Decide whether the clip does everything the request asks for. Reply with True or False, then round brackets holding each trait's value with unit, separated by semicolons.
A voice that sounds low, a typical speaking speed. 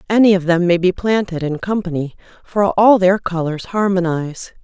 False (185 Hz; 170 wpm)